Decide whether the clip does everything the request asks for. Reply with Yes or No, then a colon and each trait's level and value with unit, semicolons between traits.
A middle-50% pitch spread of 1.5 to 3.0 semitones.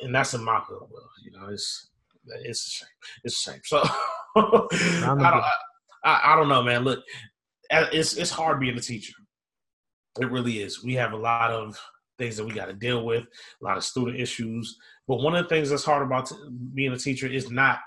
No: average, 3.7 semitones